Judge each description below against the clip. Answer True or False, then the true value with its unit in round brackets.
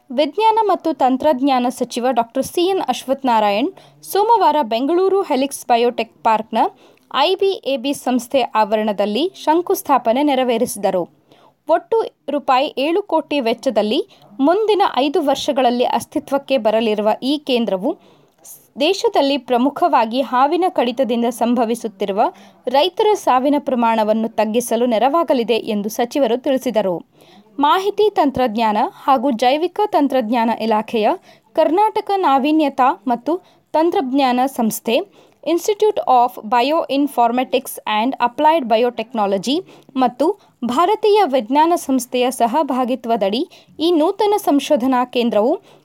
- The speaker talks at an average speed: True (90 wpm)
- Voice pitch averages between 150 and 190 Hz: False (270 Hz)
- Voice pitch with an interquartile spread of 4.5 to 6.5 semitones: True (5.2 semitones)